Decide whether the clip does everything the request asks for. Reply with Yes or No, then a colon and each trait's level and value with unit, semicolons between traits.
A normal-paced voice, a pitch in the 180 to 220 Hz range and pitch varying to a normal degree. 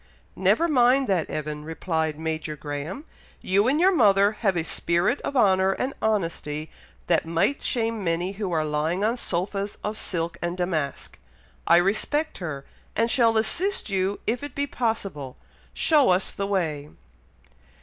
No: average, 155 wpm; high, 190 Hz; wide, 5.7 semitones